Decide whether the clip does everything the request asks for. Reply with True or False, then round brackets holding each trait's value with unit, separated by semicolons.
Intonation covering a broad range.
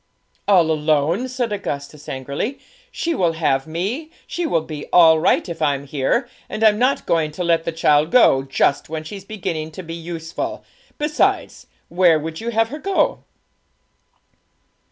True (5.8 semitones)